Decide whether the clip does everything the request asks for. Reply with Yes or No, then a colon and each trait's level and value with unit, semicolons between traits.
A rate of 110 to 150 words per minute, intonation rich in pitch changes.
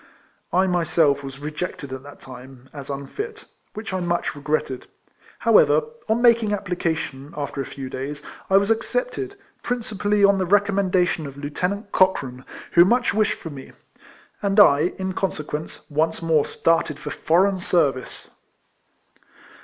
Yes: average, 145 wpm; wide, 5.8 semitones